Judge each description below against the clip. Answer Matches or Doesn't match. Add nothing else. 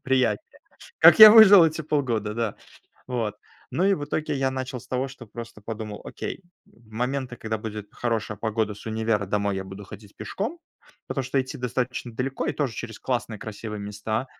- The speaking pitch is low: Matches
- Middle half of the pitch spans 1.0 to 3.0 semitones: Doesn't match